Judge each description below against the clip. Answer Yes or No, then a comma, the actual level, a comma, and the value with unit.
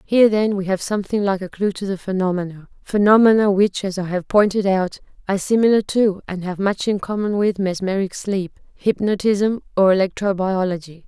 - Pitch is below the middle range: No, high, 195 Hz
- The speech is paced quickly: No, average, 175 wpm